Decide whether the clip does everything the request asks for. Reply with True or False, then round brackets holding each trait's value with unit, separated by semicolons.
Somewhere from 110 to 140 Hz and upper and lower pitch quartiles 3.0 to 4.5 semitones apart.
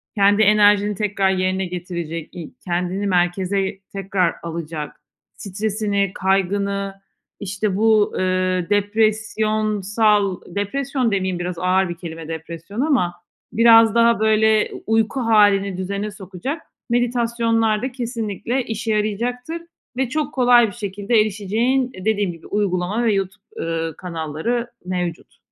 False (205 Hz; 3.3 semitones)